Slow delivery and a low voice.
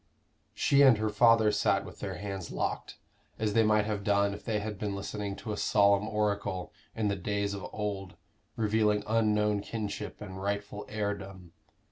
No: average, 170 wpm; low, 105 Hz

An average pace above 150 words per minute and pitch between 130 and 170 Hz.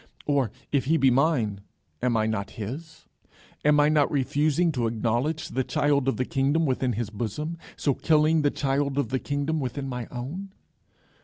Yes: average, 175 wpm; medium, 140 Hz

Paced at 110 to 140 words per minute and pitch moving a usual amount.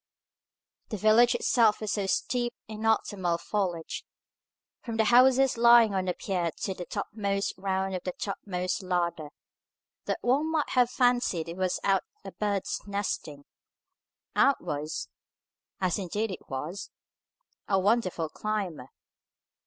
Yes: slow, 135 wpm; average, 3.8 semitones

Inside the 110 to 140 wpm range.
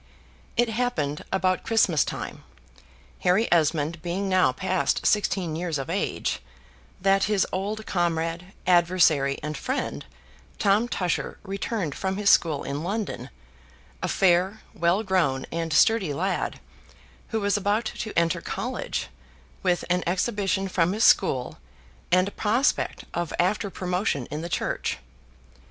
Yes: slow, 135 wpm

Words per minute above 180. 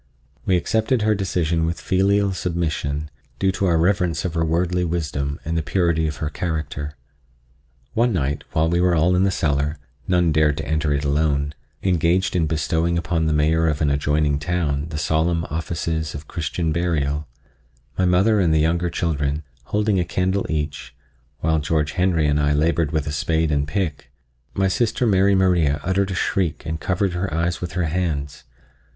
No: average, 175 wpm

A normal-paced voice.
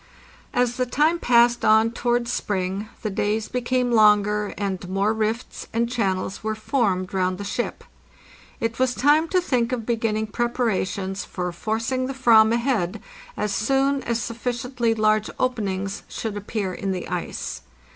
Yes: average, 155 wpm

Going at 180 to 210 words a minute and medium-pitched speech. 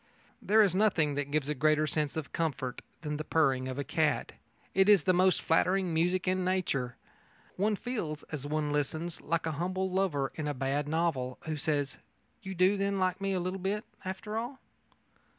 Yes: average, 185 wpm; medium, 165 Hz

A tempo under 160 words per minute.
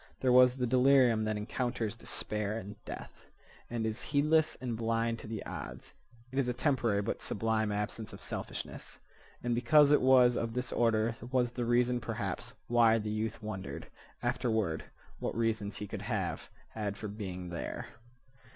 No: average, 165 wpm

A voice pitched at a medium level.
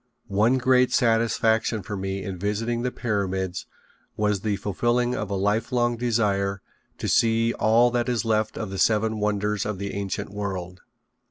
No: low, 105 Hz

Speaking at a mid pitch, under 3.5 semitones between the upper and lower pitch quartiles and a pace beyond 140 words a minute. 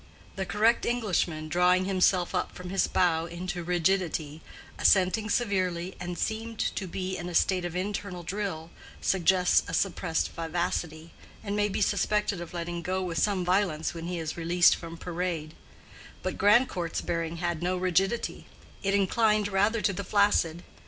Yes: medium, 180 Hz; average, 2.7 semitones; average, 160 wpm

